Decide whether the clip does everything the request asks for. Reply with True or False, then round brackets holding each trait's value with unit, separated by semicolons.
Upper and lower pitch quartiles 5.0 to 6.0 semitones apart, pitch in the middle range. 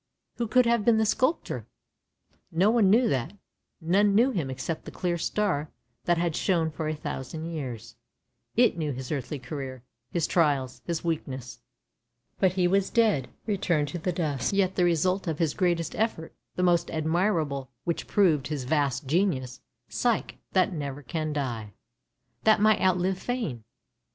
True (5.3 semitones; 165 Hz)